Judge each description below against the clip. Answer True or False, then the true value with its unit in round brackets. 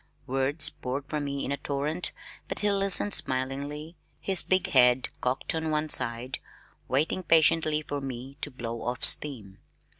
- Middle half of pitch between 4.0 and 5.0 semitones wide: False (3.4 semitones)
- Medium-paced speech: True (155 wpm)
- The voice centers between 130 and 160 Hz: True (140 Hz)